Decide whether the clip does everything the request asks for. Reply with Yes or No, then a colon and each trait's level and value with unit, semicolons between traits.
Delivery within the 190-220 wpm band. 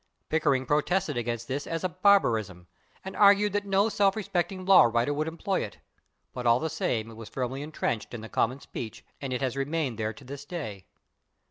Yes: average, 200 wpm